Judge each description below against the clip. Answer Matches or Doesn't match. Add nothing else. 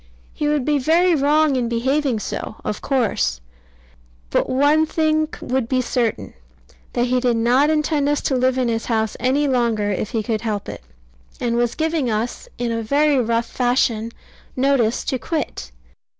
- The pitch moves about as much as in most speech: Matches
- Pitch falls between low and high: Doesn't match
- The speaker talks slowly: Doesn't match